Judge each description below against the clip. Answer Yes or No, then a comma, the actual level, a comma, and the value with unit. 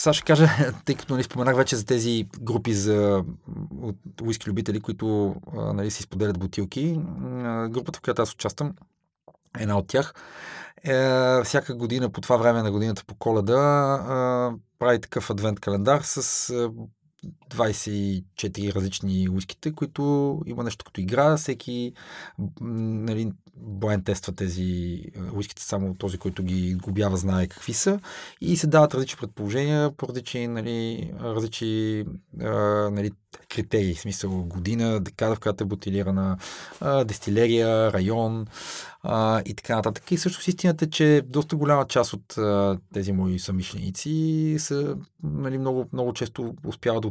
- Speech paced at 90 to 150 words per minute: Yes, average, 145 wpm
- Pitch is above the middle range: No, low, 115 Hz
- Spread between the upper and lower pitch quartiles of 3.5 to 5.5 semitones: Yes, average, 4.8 semitones